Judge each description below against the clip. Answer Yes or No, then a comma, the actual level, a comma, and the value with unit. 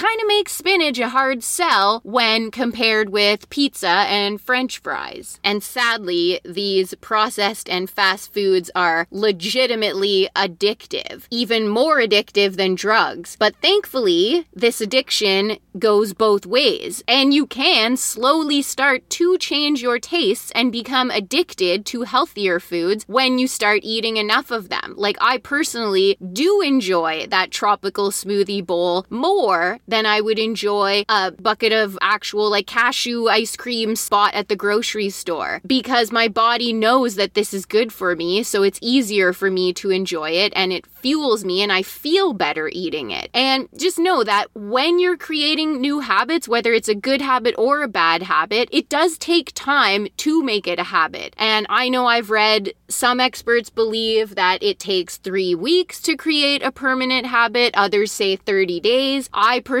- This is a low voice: No, high, 225 Hz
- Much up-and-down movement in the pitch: No, average, 4.8 semitones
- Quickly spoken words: No, average, 165 wpm